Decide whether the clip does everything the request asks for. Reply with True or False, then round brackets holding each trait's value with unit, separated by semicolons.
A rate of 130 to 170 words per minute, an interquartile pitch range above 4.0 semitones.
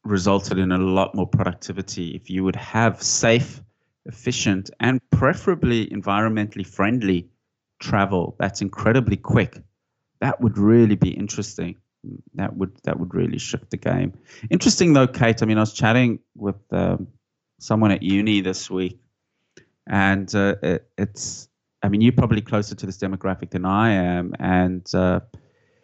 False (150 wpm; 3.5 semitones)